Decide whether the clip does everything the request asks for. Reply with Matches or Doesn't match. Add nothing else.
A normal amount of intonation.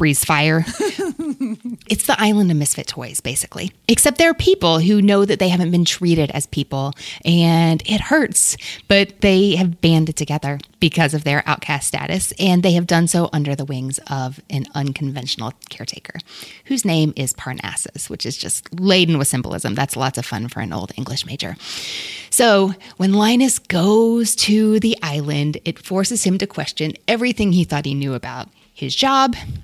Doesn't match